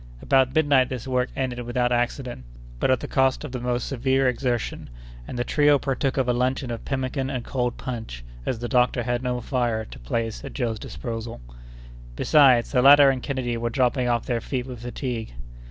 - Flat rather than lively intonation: Yes, narrow, 1.7 semitones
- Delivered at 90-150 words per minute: No, average, 195 wpm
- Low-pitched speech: Yes, low, 125 Hz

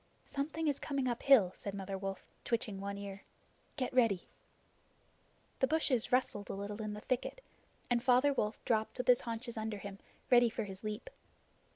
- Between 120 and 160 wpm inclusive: No, average, 170 wpm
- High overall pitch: Yes, high, 225 Hz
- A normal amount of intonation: Yes, average, 4.0 semitones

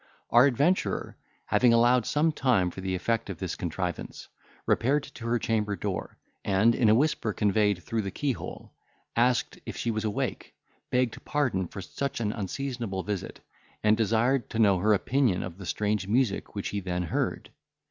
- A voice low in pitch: Yes, low, 110 Hz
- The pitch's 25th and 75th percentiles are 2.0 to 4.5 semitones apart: Yes, average, 4.1 semitones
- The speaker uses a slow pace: No, average, 170 wpm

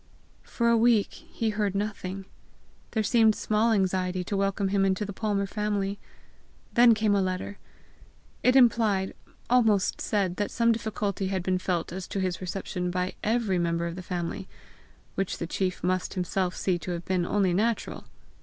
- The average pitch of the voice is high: Yes, high, 195 Hz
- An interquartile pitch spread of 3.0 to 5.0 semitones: No, narrow, 2.6 semitones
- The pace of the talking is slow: No, average, 170 wpm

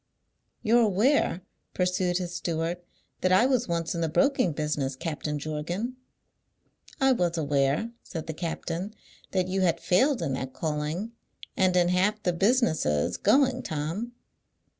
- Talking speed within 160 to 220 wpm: No, average, 140 wpm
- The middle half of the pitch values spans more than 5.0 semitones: Yes, wide, 5.4 semitones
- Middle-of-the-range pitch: Yes, medium, 180 Hz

